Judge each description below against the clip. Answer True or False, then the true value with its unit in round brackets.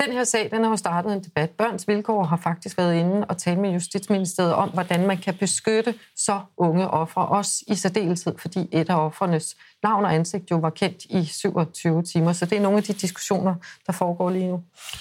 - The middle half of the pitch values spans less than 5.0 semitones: True (2.9 semitones)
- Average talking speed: True (215 wpm)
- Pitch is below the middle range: False (185 Hz)